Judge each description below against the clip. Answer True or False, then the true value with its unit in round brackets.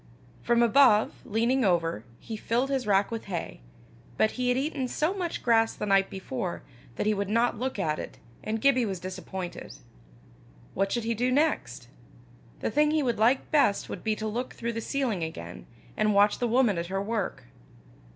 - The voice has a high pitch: True (225 Hz)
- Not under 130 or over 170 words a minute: False (190 wpm)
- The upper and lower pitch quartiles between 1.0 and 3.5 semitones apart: False (4.3 semitones)